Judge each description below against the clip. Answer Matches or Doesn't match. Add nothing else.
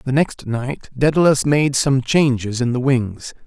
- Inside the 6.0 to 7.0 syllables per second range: Doesn't match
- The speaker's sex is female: Doesn't match